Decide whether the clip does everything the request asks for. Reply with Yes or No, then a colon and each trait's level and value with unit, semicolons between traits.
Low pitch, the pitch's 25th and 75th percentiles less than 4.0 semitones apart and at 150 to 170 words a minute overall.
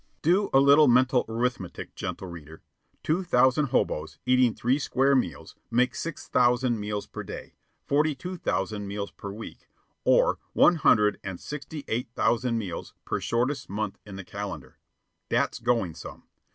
No: low, 120 Hz; average, 5.1 semitones; average, 155 wpm